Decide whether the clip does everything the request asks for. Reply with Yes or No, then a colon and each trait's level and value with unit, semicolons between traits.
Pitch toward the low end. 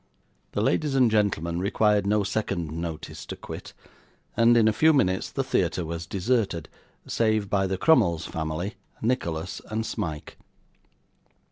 Yes: low, 100 Hz